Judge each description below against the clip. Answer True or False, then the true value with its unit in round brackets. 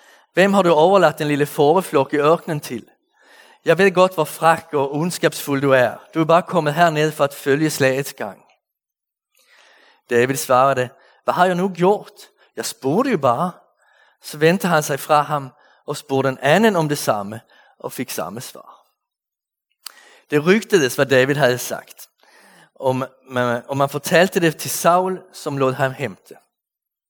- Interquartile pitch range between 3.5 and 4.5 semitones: True (3.8 semitones)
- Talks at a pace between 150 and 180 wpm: True (170 wpm)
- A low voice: False (150 Hz)